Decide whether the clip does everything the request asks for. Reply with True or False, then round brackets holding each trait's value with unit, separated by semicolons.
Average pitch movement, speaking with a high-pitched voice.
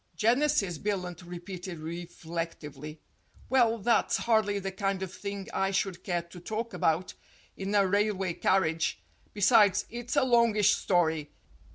True (3.5 semitones; 195 Hz)